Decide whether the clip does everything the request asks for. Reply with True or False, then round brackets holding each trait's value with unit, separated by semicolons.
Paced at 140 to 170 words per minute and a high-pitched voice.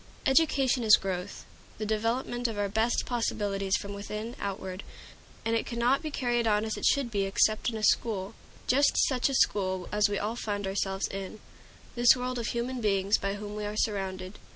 False (190 wpm; 215 Hz)